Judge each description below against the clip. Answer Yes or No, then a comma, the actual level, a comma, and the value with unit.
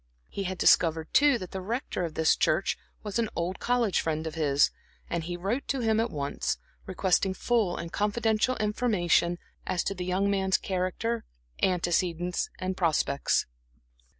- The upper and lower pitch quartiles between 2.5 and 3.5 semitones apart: No, average, 4.0 semitones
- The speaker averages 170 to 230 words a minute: No, average, 160 wpm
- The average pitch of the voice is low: No, medium, 185 Hz